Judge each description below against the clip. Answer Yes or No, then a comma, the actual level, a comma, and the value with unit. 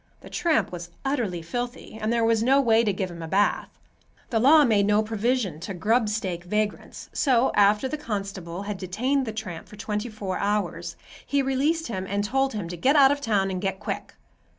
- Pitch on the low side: No, high, 215 Hz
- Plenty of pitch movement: No, average, 4.5 semitones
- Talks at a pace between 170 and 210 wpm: Yes, average, 200 wpm